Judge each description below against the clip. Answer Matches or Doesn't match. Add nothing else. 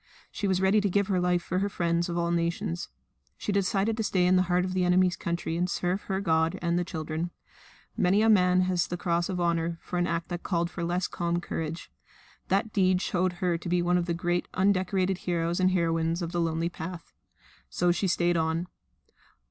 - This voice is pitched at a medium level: Matches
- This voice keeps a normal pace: Doesn't match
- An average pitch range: Doesn't match